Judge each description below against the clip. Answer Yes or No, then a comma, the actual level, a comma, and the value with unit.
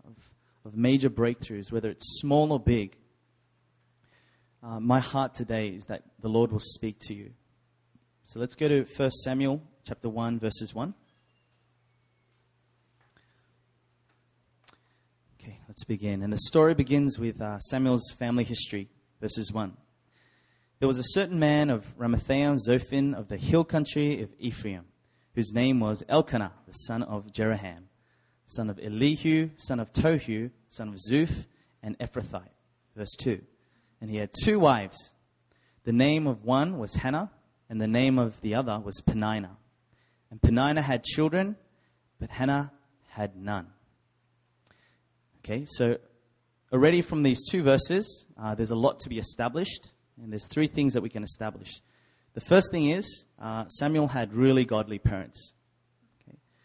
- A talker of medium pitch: No, low, 120 Hz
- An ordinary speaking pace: Yes, average, 145 wpm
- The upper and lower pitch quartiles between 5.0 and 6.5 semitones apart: No, average, 3.7 semitones